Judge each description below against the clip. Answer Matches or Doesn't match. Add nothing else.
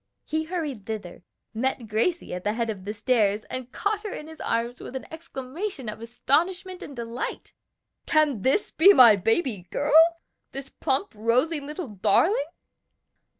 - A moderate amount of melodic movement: Doesn't match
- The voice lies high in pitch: Matches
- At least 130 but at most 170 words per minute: Matches